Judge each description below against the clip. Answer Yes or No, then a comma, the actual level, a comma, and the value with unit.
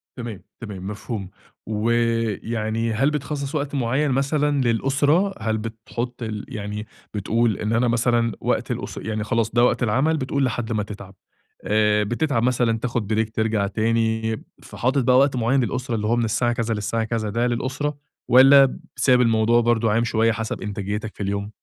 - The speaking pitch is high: No, low, 115 Hz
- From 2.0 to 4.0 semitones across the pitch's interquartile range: Yes, average, 2.8 semitones